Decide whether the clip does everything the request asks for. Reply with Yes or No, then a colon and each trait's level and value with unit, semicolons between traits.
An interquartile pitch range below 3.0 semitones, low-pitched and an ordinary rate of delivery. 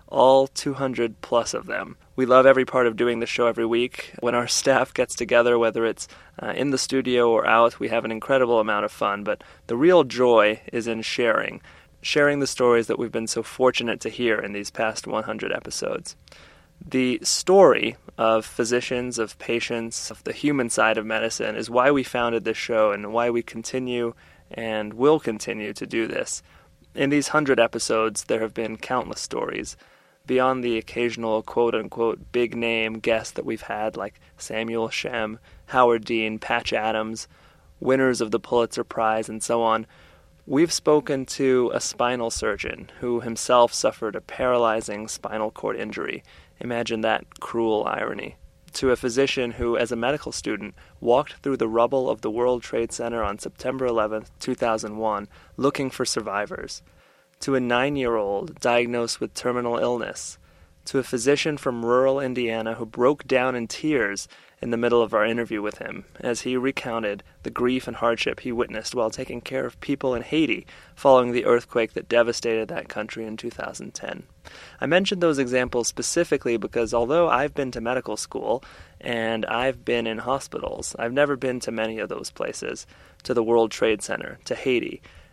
Yes: narrow, 2.4 semitones; low, 120 Hz; average, 175 wpm